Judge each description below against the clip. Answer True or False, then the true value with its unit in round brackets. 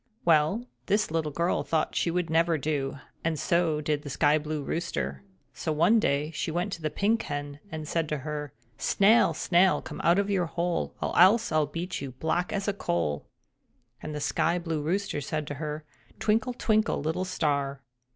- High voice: False (160 Hz)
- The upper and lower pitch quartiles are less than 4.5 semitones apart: True (3.3 semitones)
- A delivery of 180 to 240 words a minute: True (190 wpm)